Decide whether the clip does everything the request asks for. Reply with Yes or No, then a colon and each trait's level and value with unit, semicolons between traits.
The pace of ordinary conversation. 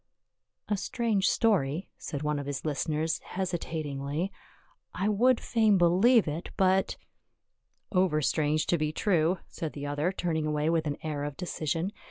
Yes: average, 175 wpm